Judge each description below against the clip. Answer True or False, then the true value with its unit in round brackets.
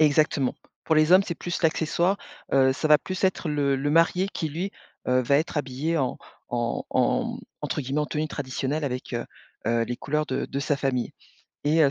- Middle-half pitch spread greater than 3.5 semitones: False (3.2 semitones)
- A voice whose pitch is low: False (145 Hz)